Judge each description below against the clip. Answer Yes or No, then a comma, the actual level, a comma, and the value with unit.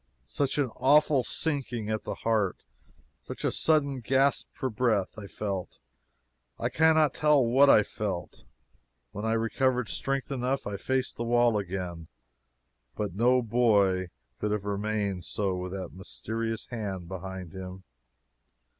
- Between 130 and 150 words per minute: Yes, average, 140 wpm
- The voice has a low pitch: Yes, low, 110 Hz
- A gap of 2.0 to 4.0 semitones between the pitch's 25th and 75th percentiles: No, average, 5.1 semitones